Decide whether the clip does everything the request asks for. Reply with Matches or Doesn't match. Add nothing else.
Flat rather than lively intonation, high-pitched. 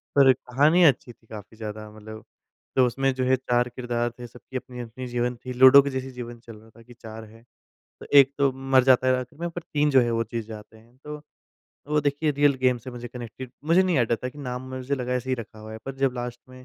Doesn't match